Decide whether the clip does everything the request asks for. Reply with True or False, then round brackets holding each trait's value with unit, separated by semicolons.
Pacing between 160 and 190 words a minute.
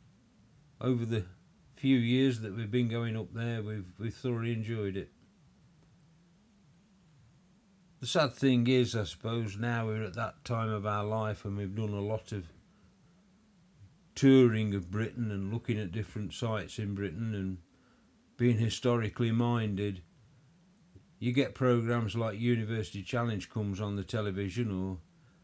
False (140 wpm)